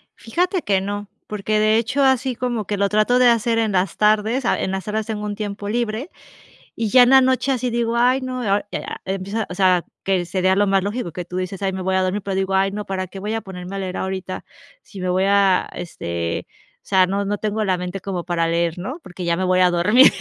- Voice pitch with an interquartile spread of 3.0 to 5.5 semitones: Yes, average, 3.3 semitones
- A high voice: Yes, high, 200 Hz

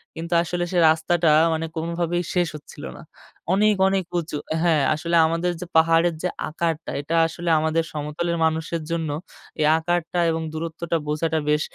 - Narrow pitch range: Yes, narrow, 1.4 semitones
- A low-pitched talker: No, medium, 165 Hz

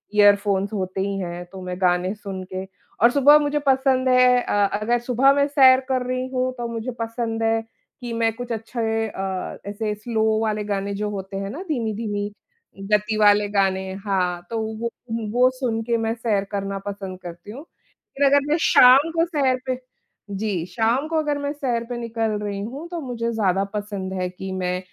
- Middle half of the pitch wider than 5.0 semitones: No, average, 4.1 semitones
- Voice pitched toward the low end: No, high, 220 Hz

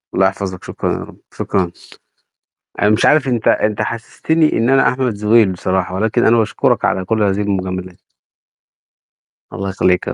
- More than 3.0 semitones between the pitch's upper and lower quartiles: Yes, average, 3.6 semitones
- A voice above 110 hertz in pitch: No, low, 105 Hz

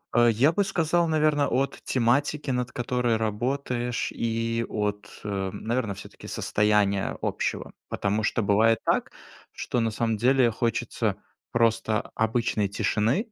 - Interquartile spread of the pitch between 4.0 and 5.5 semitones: No, average, 3.1 semitones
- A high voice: No, low, 115 Hz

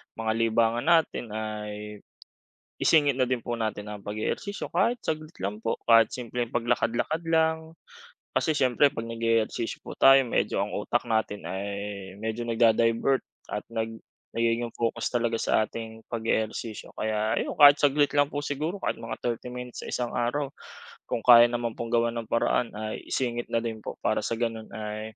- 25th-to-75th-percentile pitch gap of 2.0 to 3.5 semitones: Yes, narrow, 2.5 semitones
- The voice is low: Yes, low, 115 Hz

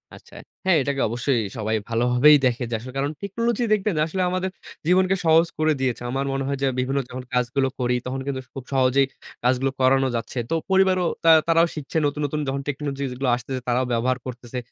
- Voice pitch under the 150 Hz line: Yes, low, 135 Hz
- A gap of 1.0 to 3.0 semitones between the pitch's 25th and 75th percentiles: No, average, 3.9 semitones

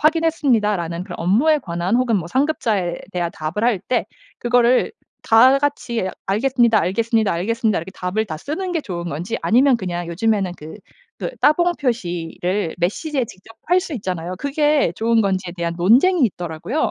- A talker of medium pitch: No, high, 220 Hz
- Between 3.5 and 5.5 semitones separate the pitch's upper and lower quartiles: No, wide, 6.9 semitones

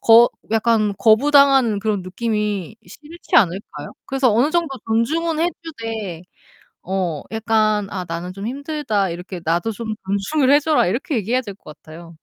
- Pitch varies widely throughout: Yes, wide, 5.8 semitones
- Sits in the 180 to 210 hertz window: No, high, 220 Hz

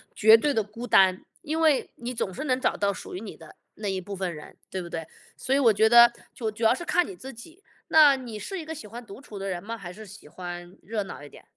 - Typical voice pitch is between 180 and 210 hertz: No, high, 220 Hz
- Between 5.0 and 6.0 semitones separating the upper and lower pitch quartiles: Yes, average, 5.3 semitones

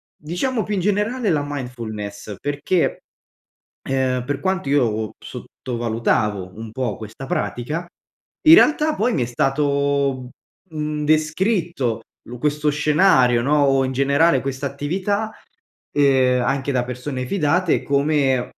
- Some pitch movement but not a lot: Yes, average, 4.2 semitones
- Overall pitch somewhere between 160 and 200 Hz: No, medium, 140 Hz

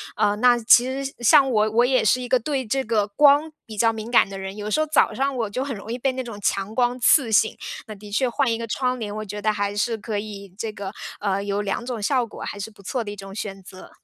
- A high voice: Yes, high, 220 Hz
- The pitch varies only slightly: No, average, 3.6 semitones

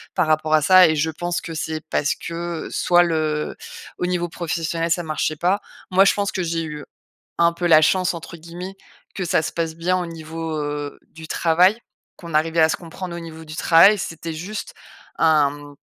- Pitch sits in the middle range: Yes, medium, 165 Hz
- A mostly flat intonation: Yes, narrow, 1.9 semitones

